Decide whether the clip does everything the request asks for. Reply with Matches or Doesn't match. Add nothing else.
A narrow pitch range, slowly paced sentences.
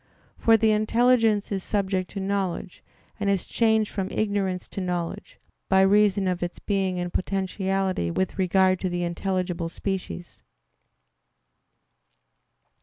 Matches